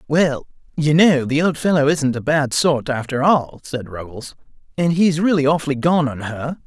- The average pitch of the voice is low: No, medium, 145 Hz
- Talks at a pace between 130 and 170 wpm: No, average, 190 wpm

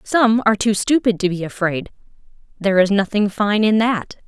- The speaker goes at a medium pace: Yes, average, 185 wpm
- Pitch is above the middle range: Yes, high, 210 Hz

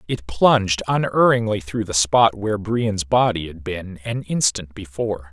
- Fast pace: No, average, 160 wpm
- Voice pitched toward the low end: Yes, low, 100 Hz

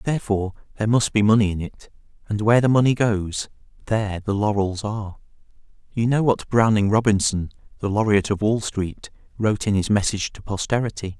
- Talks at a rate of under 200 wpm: Yes, average, 170 wpm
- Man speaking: Yes, male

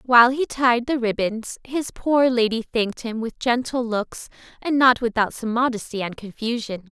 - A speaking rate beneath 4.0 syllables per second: No, 4.8 syllables/s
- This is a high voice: Yes, high, 235 Hz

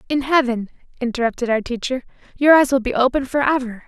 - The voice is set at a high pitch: Yes, very high, 255 Hz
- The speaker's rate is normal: Yes, average, 170 wpm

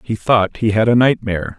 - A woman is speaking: No, male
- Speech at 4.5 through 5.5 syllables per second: Yes, 5.4 syllables/s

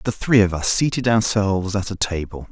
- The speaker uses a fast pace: Yes, fast, 215 wpm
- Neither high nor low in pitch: No, low, 100 Hz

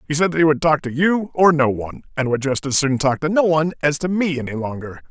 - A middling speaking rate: No, fast, 295 wpm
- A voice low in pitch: No, medium, 150 Hz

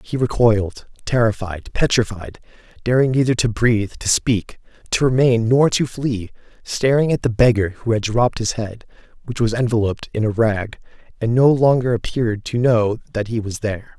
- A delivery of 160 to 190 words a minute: Yes, average, 170 wpm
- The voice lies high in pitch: No, low, 115 Hz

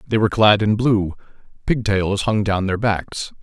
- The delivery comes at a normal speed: Yes, average, 175 wpm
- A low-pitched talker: Yes, low, 105 Hz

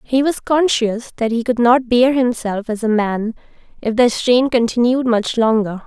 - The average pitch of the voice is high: Yes, high, 235 Hz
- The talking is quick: No, average, 185 wpm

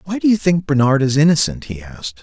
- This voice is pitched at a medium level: Yes, medium, 150 Hz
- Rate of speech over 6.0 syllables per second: Yes, 6.2 syllables/s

